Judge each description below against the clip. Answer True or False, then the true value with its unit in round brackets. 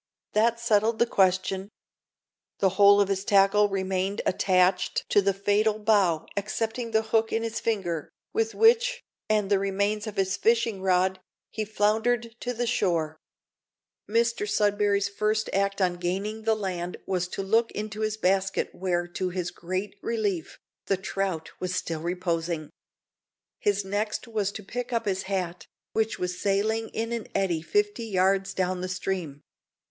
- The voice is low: False (200 Hz)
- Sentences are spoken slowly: False (155 wpm)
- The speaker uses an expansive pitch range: False (2.8 semitones)